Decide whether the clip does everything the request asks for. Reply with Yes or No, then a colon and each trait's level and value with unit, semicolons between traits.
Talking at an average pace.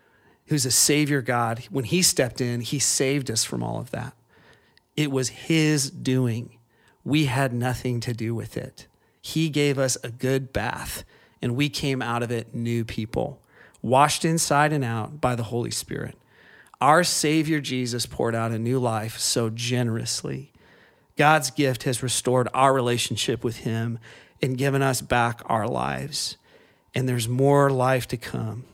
Yes: average, 165 wpm